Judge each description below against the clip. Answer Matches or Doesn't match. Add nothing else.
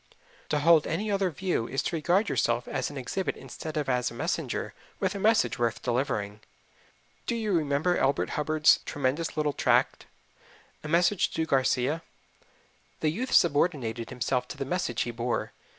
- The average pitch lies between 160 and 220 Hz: Doesn't match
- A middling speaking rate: Matches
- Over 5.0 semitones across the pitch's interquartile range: Matches